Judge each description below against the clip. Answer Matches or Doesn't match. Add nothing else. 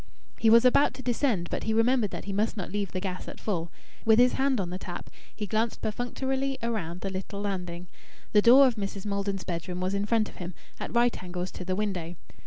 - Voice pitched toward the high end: Matches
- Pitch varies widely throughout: Doesn't match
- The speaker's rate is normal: Doesn't match